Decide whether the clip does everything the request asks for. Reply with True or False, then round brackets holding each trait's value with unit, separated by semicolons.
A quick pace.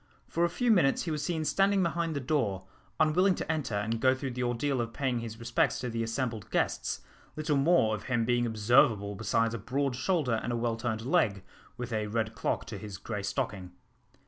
True (210 wpm)